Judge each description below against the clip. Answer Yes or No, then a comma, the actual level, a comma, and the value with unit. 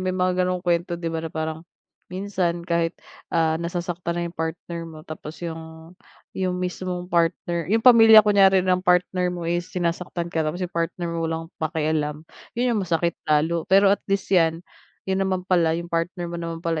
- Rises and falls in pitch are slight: Yes, narrow, 1.9 semitones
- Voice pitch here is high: No, medium, 170 Hz